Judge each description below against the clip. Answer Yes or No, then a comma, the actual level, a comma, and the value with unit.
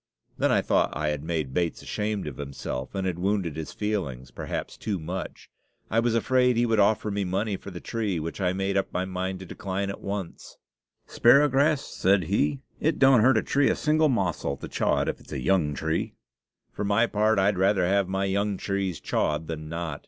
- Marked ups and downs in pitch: No, average, 4.2 semitones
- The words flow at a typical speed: No, fast, 210 wpm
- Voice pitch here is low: Yes, very low, 95 Hz